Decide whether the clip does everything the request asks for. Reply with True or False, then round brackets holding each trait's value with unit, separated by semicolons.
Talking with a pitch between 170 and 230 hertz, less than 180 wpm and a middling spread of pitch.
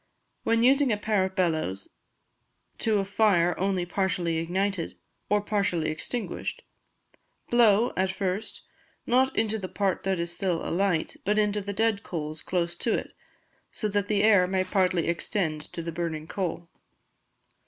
True (190 Hz; 155 wpm; 3.4 semitones)